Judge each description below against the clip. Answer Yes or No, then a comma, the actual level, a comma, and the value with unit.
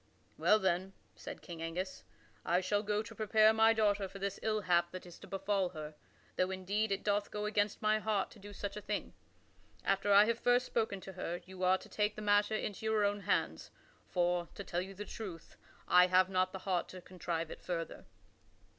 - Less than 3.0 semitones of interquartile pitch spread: Yes, narrow, 2.4 semitones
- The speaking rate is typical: No, fast, 210 wpm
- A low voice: No, high, 195 Hz